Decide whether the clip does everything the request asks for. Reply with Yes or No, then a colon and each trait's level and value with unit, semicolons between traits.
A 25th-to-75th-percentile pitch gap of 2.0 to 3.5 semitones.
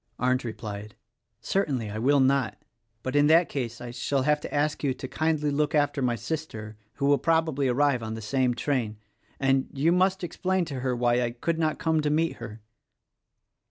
No: average, 4.0 semitones